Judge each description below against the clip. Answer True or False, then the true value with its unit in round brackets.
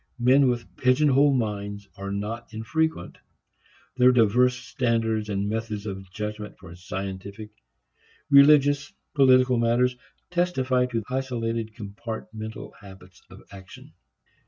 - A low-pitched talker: True (115 Hz)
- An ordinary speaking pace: False (110 wpm)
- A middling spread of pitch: True (3.8 semitones)